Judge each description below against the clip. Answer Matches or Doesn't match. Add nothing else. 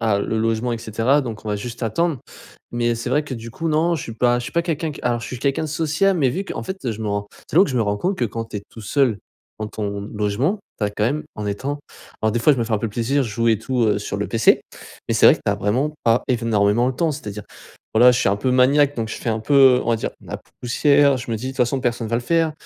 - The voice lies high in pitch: Doesn't match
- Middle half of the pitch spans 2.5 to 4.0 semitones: Doesn't match